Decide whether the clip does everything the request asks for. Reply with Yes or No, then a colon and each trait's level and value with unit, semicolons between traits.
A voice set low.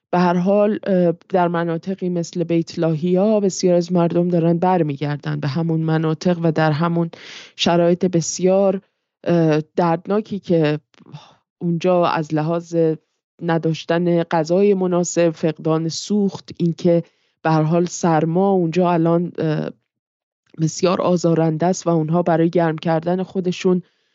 No: medium, 170 Hz